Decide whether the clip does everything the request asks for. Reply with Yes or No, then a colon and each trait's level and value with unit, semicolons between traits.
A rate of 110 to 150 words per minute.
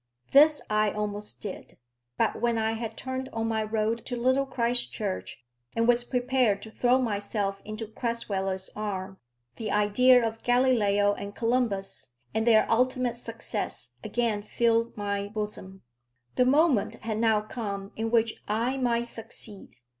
Yes: average, 145 wpm